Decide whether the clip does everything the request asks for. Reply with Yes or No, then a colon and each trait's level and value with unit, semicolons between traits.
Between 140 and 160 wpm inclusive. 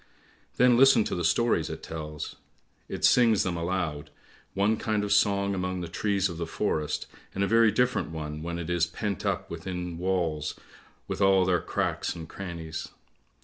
No: average, 175 wpm